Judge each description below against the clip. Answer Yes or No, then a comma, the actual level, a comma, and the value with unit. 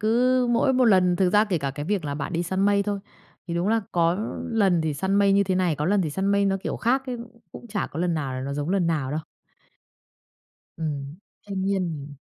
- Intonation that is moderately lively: Yes, average, 4.4 semitones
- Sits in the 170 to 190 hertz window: Yes, medium, 185 Hz